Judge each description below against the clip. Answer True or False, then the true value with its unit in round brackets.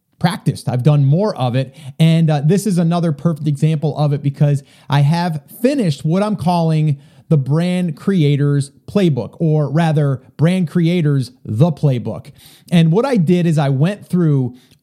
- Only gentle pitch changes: False (3.4 semitones)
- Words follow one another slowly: False (160 wpm)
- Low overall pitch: False (155 Hz)